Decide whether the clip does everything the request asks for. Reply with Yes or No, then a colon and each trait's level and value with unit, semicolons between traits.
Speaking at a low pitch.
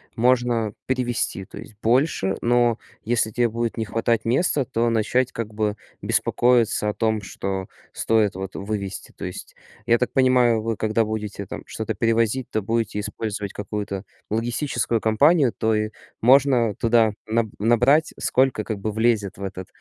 Yes: low, 115 Hz